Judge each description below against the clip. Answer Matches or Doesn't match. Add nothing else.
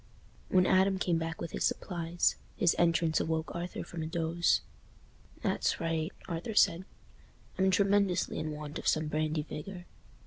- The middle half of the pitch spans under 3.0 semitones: Matches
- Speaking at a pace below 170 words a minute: Matches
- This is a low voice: Doesn't match